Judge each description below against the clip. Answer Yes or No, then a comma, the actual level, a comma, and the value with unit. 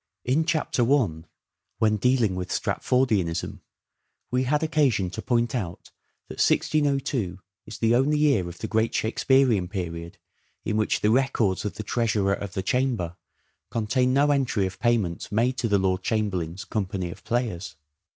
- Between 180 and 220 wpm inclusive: No, average, 155 wpm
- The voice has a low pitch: Yes, low, 110 Hz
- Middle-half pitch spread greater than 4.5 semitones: Yes, wide, 5.4 semitones